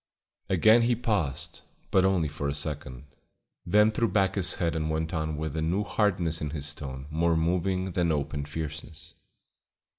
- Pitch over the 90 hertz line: No, very low, 80 Hz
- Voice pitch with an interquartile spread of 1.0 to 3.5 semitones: No, average, 3.9 semitones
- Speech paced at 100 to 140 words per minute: No, average, 170 wpm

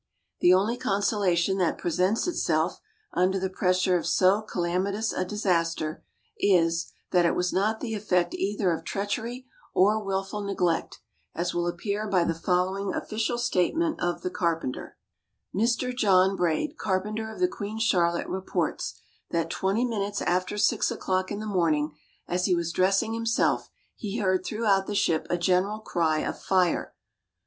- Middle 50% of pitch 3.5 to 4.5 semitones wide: No, average, 3.0 semitones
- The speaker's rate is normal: Yes, average, 155 wpm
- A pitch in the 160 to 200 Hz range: Yes, high, 190 Hz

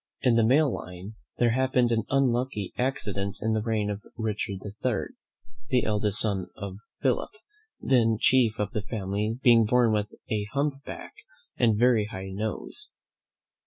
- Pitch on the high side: No, low, 110 Hz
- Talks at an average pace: Yes, average, 155 wpm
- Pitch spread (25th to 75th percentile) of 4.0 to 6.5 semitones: No, average, 3.1 semitones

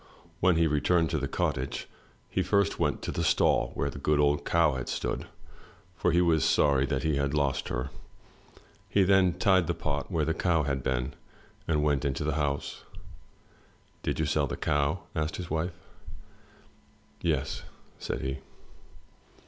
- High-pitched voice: No, very low, 75 Hz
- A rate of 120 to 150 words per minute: No, average, 170 wpm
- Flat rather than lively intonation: No, average, 3.1 semitones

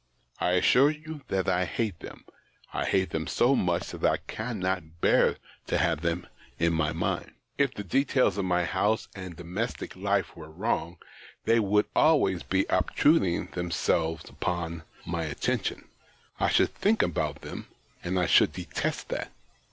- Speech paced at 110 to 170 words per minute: Yes, average, 160 wpm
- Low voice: Yes, very low, 90 Hz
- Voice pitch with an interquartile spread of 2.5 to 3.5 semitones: No, average, 4.6 semitones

